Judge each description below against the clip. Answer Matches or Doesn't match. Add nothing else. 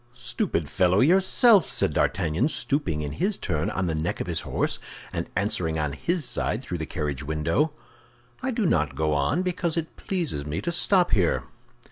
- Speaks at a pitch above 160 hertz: Doesn't match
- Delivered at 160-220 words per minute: Matches